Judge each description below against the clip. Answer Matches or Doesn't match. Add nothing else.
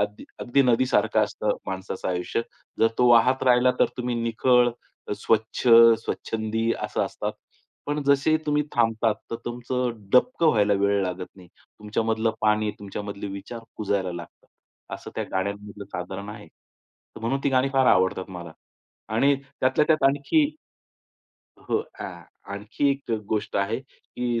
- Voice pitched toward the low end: Matches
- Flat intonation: Doesn't match